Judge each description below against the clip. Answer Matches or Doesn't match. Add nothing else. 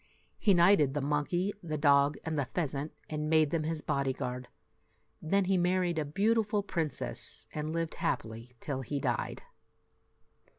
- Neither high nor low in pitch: Matches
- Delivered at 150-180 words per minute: Matches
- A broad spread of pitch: Doesn't match